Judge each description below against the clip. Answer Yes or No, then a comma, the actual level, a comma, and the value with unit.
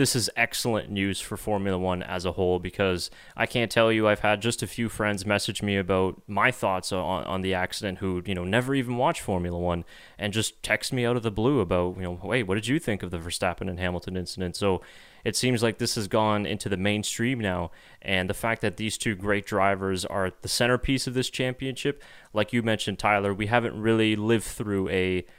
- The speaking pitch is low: Yes, low, 105 Hz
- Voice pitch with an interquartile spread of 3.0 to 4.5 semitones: Yes, average, 3.7 semitones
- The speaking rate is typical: No, fast, 225 wpm